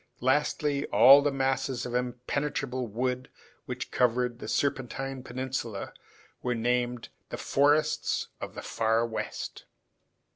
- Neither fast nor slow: No, slow, 115 wpm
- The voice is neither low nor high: No, low, 125 Hz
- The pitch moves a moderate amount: No, narrow, 2.0 semitones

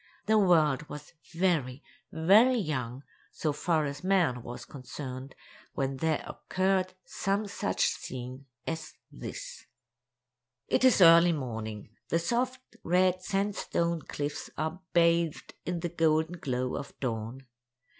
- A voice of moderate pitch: Yes, medium, 160 Hz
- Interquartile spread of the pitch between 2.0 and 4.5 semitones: No, wide, 5.5 semitones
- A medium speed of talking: No, slow, 125 wpm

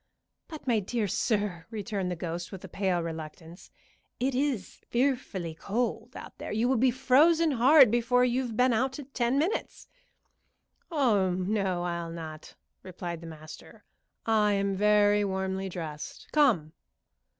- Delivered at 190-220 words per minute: No, average, 140 wpm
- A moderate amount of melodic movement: No, wide, 5.9 semitones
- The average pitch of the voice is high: Yes, high, 205 Hz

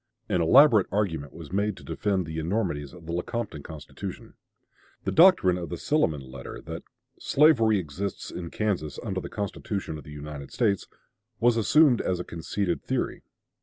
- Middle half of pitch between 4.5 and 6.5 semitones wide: Yes, average, 5.3 semitones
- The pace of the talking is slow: No, average, 165 wpm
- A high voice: No, very low, 90 Hz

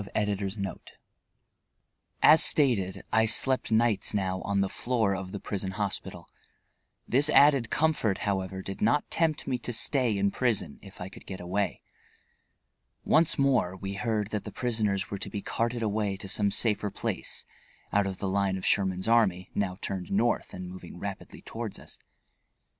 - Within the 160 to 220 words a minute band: Yes, average, 165 wpm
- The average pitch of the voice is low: Yes, low, 100 Hz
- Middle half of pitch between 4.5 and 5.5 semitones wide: No, average, 3.4 semitones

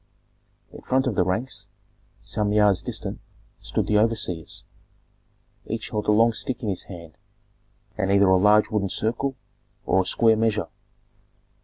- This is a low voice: Yes, low, 105 Hz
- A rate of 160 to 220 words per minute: No, average, 150 wpm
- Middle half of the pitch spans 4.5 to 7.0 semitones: No, average, 3.1 semitones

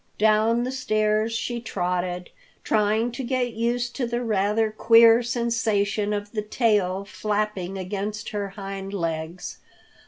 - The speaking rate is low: Yes, slow, 130 wpm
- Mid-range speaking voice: No, high, 215 Hz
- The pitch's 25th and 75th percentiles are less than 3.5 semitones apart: Yes, average, 2.8 semitones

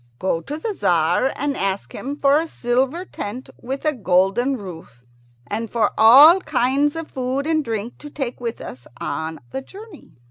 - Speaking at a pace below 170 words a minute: No, average, 175 wpm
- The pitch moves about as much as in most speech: No, wide, 6.3 semitones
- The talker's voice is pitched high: Yes, very high, 255 Hz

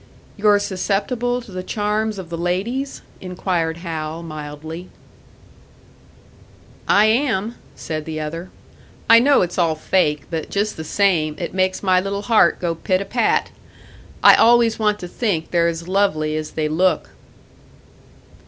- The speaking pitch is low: No, medium, 185 Hz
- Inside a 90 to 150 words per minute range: Yes, average, 145 wpm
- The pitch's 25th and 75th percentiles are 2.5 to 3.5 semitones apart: No, average, 4.2 semitones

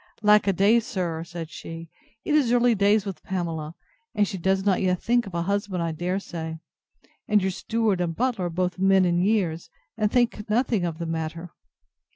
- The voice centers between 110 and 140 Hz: No, high, 190 Hz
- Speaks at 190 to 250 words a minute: Yes, average, 195 wpm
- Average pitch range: Yes, average, 3.7 semitones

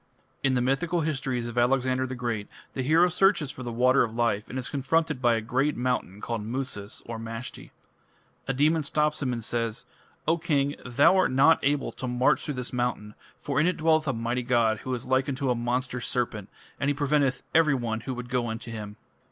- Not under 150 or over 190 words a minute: No, fast, 205 wpm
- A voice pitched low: Yes, low, 130 Hz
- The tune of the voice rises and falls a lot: No, average, 3.1 semitones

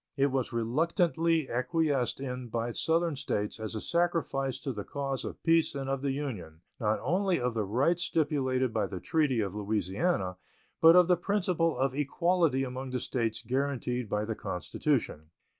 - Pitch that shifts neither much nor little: No, wide, 6.0 semitones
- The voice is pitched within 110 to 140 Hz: Yes, low, 135 Hz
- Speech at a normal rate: Yes, average, 170 wpm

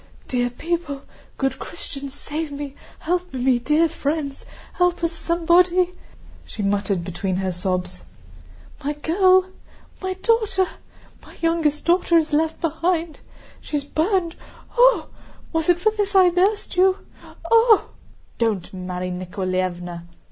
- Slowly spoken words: Yes, slow, 125 wpm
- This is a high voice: Yes, very high, 320 Hz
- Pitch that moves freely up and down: Yes, wide, 6.9 semitones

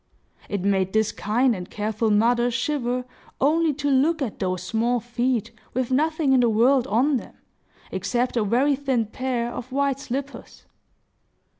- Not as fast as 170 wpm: Yes, average, 155 wpm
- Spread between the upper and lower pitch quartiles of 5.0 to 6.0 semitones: No, average, 3.7 semitones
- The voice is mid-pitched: No, high, 245 Hz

